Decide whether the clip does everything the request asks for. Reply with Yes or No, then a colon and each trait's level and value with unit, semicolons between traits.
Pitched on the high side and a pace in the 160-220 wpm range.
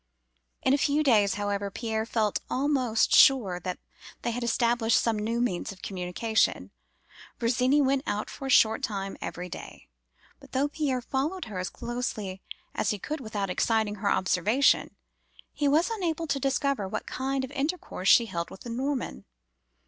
Yes: high, 235 Hz; average, 165 wpm